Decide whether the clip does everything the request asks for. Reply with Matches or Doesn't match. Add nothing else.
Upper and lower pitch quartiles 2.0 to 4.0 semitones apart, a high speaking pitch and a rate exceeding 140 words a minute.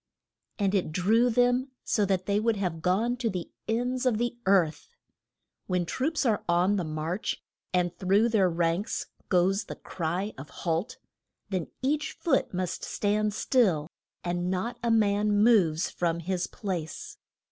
Doesn't match